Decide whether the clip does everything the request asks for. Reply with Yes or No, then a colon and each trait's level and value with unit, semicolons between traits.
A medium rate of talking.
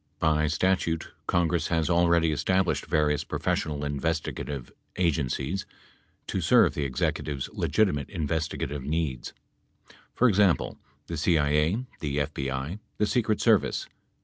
No: slow, 115 wpm